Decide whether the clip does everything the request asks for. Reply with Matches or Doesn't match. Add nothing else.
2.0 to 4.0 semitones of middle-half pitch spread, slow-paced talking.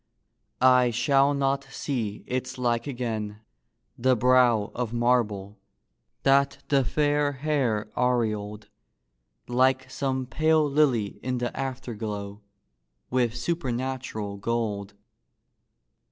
Matches